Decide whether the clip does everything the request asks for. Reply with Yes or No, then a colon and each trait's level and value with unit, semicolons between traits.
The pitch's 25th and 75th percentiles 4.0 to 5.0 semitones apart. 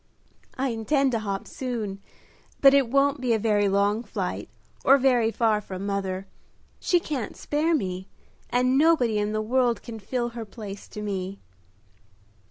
Yes: average, 4.3 semitones